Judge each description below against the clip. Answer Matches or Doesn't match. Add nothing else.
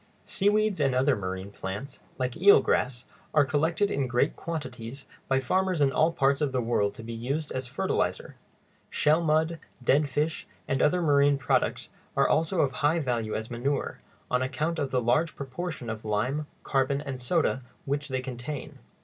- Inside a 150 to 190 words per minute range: Matches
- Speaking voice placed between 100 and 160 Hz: Matches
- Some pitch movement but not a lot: Matches